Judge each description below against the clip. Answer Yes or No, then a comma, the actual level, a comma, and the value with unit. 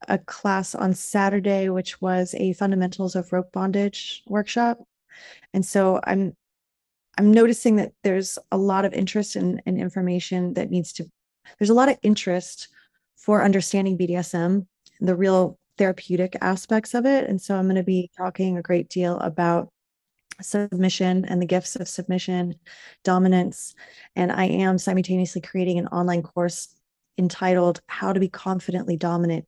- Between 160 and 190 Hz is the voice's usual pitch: Yes, medium, 185 Hz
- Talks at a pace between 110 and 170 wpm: Yes, average, 155 wpm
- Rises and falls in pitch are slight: Yes, narrow, 1.5 semitones